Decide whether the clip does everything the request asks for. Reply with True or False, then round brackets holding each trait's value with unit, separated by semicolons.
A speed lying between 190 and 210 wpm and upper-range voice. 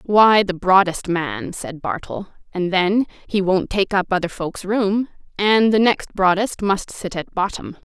False (175 wpm; 195 Hz)